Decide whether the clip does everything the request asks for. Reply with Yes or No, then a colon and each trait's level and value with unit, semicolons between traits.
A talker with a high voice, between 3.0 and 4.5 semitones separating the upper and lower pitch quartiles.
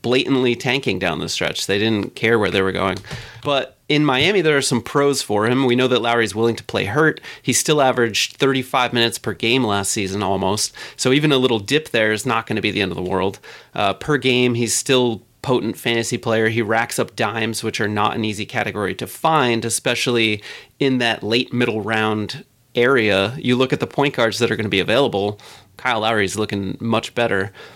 No: low, 115 Hz; average, 3.3 semitones